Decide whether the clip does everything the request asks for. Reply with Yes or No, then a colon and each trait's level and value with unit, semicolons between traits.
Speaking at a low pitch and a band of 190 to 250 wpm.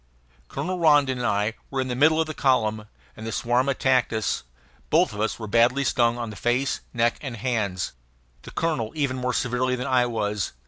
Yes: low, 125 Hz; average, 200 wpm